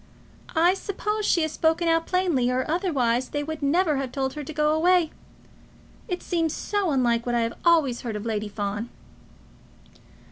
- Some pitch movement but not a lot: No, wide, 5.8 semitones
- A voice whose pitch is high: Yes, very high, 300 Hz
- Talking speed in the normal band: Yes, average, 175 wpm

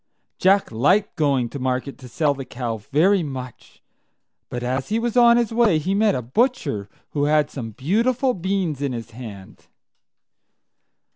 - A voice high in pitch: No, medium, 145 Hz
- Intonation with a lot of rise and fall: Yes, wide, 7.9 semitones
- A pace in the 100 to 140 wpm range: No, average, 160 wpm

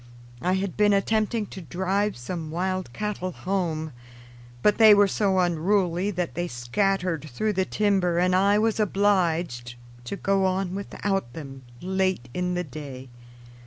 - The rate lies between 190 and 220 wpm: No, average, 150 wpm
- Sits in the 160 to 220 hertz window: Yes, medium, 185 Hz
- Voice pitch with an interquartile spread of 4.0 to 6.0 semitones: No, average, 3.1 semitones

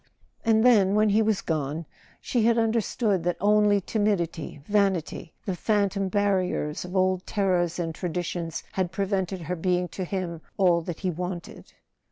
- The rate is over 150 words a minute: Yes, average, 160 wpm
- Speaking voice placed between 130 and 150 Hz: No, medium, 185 Hz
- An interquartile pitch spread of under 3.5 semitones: Yes, average, 2.8 semitones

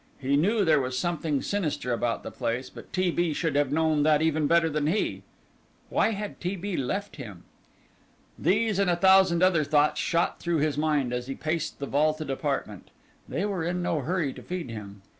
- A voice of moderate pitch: Yes, medium, 155 Hz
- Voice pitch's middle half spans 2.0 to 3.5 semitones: No, average, 4.0 semitones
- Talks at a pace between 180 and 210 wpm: Yes, average, 195 wpm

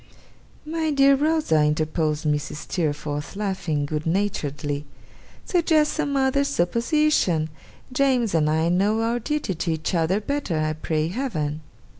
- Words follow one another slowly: Yes, slow, 130 wpm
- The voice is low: No, medium, 180 Hz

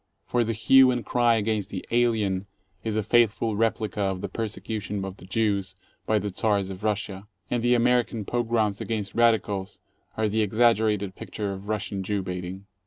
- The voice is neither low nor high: No, low, 105 Hz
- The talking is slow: No, average, 175 wpm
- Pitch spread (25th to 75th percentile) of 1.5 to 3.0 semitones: Yes, narrow, 2.6 semitones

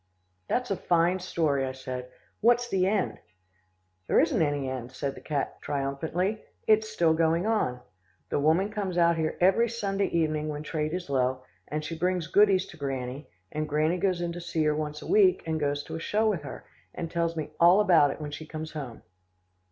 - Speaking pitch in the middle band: Yes, medium, 160 Hz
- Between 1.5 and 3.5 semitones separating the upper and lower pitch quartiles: No, average, 4.0 semitones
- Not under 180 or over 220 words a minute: Yes, fast, 205 wpm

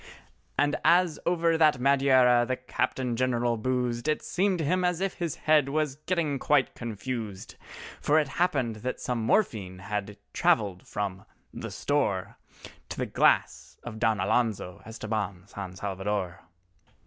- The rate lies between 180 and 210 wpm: No, average, 145 wpm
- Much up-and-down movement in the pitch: Yes, wide, 6.4 semitones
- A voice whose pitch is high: No, low, 125 Hz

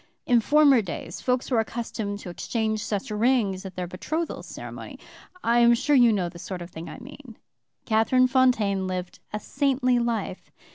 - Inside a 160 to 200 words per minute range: Yes, average, 175 wpm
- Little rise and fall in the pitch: No, average, 4.7 semitones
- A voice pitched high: Yes, high, 225 Hz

